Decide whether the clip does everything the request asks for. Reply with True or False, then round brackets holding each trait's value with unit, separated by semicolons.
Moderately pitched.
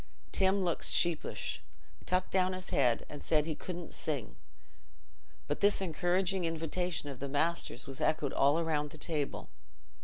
True (165 Hz)